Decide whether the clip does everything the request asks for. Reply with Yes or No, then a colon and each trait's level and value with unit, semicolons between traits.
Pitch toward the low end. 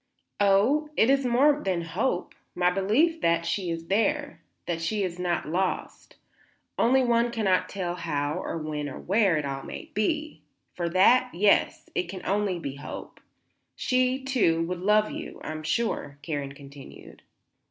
No: medium, 185 Hz